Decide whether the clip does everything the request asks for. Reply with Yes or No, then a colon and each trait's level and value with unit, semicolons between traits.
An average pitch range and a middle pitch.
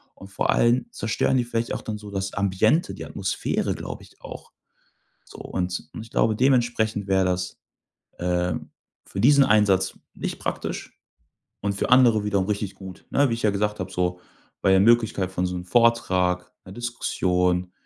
No: average, 4.1 semitones; low, 100 Hz